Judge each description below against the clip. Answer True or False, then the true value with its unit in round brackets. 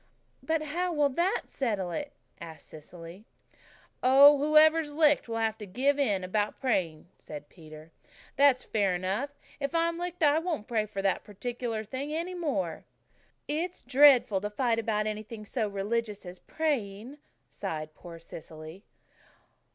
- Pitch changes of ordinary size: False (7.1 semitones)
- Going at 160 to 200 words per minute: False (150 wpm)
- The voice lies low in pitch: False (230 Hz)